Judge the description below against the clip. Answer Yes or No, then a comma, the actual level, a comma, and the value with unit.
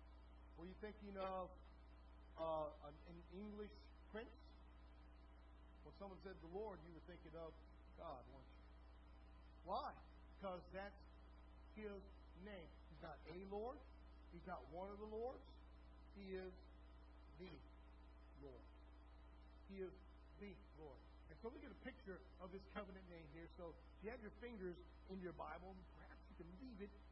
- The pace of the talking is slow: No, average, 155 wpm